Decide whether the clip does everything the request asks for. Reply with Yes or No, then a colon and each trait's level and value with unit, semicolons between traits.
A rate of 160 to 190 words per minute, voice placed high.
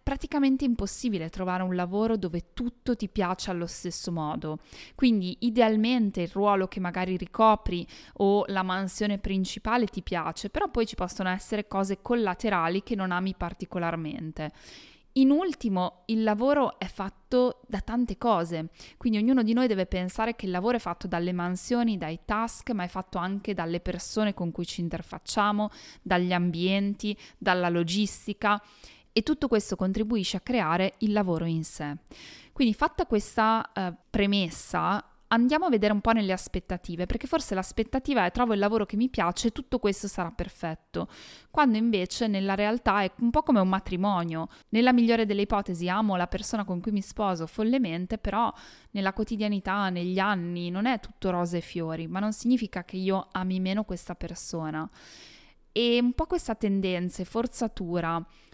Yes: average, 165 wpm; high, 200 Hz